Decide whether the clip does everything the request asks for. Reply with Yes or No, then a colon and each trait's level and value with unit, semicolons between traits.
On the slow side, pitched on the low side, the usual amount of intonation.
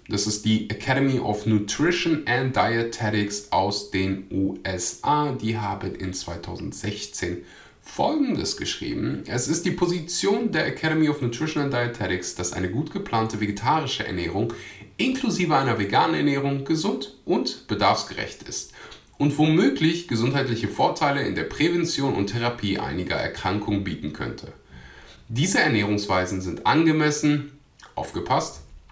No: slow, 120 wpm; low, 115 Hz; wide, 6.7 semitones